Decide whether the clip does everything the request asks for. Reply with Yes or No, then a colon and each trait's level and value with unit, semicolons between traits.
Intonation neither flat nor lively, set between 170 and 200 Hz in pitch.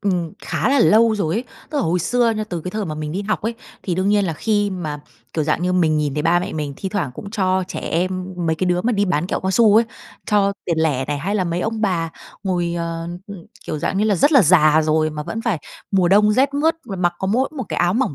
Yes: average, 4.3 semitones; medium, 185 Hz